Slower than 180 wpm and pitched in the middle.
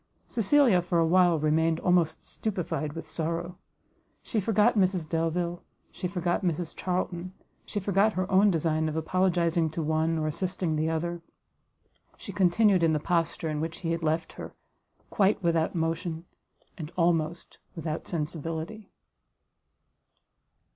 Yes: average, 140 wpm; medium, 170 Hz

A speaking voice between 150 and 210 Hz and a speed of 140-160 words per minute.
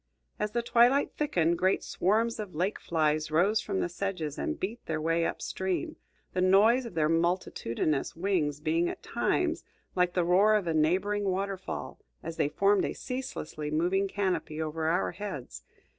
No: medium, 185 Hz; average, 170 wpm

